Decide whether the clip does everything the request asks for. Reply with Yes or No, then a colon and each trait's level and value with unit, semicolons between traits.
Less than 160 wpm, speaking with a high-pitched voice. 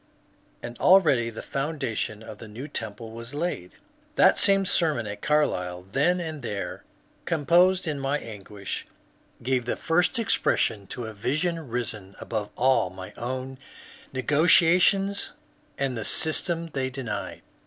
No: slow, 135 wpm; low, 130 Hz